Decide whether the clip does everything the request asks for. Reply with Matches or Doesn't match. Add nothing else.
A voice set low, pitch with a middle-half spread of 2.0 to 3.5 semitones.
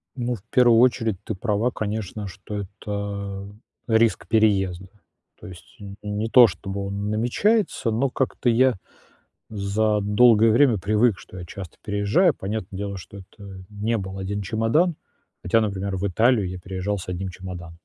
Matches